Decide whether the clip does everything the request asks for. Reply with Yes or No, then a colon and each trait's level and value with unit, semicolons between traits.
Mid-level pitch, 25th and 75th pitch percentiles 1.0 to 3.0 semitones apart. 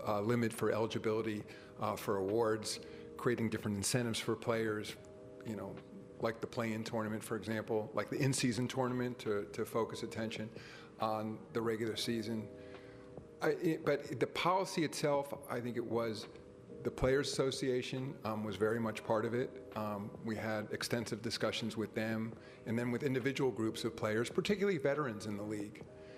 No: low, 115 Hz; narrow, 2.4 semitones